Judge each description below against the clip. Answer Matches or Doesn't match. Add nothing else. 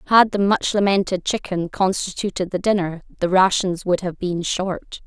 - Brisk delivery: Doesn't match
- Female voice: Matches